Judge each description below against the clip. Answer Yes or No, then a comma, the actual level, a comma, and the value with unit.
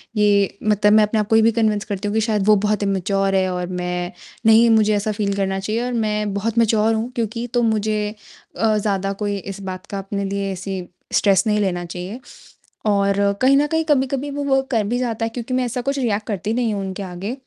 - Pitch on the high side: Yes, high, 210 Hz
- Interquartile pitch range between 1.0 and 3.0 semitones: Yes, narrow, 2.4 semitones